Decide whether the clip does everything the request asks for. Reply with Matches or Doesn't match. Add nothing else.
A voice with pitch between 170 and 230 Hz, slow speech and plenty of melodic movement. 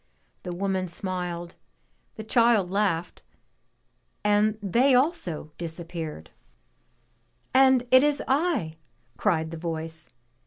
Matches